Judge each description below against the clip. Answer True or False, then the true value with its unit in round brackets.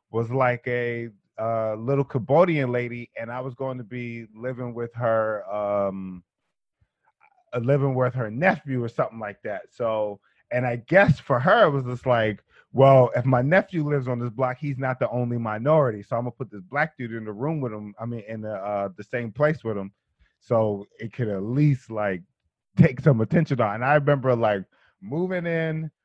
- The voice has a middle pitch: False (125 Hz)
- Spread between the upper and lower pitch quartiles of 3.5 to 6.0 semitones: True (3.9 semitones)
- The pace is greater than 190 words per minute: True (200 wpm)